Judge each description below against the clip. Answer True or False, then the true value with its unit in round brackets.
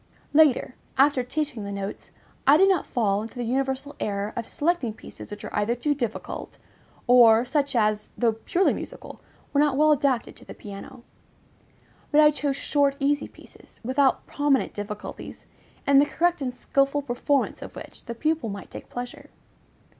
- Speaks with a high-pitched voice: True (265 Hz)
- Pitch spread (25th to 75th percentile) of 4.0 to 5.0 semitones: True (4.3 semitones)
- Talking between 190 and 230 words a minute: False (170 wpm)